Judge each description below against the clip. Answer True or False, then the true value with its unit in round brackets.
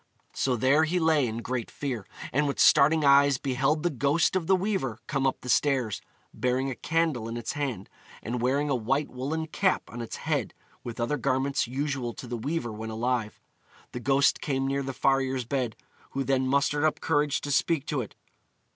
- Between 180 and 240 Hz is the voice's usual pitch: False (135 Hz)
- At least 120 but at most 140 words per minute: False (195 wpm)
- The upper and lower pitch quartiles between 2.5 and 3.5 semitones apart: True (3.0 semitones)